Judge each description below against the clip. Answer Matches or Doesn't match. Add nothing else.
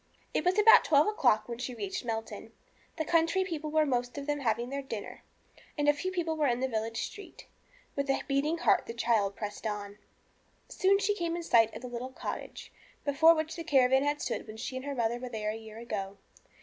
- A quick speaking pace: Matches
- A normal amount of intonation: Doesn't match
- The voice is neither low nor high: Doesn't match